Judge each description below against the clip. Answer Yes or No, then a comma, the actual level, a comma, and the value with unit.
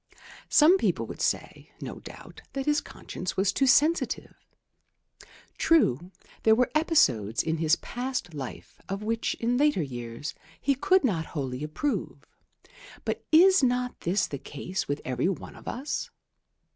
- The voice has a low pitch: No, high, 215 Hz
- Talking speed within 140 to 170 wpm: Yes, average, 145 wpm